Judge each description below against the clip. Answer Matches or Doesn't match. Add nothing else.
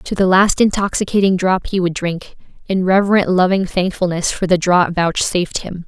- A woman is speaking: Matches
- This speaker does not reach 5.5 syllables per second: Matches